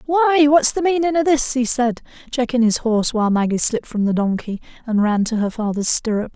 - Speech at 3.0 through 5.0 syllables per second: No, 5.7 syllables/s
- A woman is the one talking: Yes, female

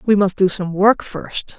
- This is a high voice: Yes, high, 195 Hz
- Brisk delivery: Yes, fast, 225 wpm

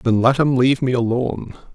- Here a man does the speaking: Yes, male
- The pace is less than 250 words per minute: Yes, fast, 205 wpm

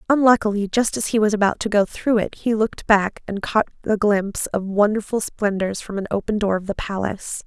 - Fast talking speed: Yes, fast, 215 wpm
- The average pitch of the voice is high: Yes, high, 210 Hz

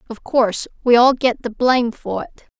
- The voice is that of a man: No, female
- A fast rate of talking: Yes, fast, 210 wpm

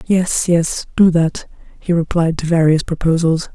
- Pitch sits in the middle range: Yes, medium, 165 Hz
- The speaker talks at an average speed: Yes, average, 150 wpm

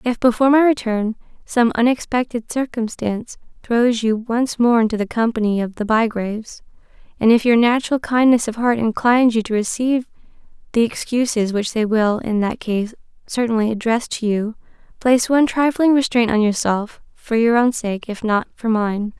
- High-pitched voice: Yes, high, 230 Hz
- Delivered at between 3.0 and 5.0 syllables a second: No, 5.2 syllables/s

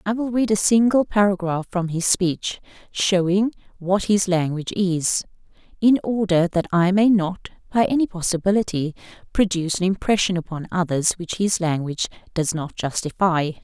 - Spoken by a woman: Yes, female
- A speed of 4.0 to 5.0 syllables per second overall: Yes, 4.9 syllables/s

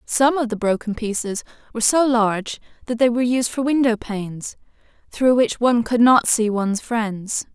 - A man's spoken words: No, female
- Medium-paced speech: Yes, average, 175 wpm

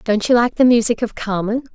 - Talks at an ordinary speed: No, fast, 240 wpm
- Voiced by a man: No, female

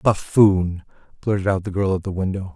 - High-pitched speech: No, very low, 95 Hz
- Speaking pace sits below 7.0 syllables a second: Yes, 5.2 syllables/s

